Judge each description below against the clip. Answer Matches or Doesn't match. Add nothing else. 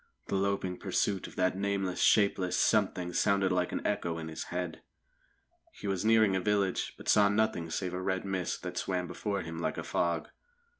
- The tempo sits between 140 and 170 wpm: Doesn't match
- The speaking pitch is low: Matches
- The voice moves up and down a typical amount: Doesn't match